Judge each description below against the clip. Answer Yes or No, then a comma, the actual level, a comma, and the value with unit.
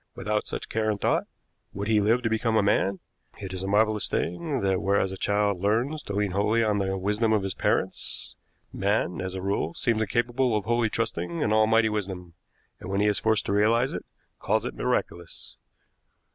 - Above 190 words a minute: Yes, average, 200 wpm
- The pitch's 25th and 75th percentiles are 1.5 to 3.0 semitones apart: Yes, narrow, 2.4 semitones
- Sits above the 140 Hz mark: No, low, 105 Hz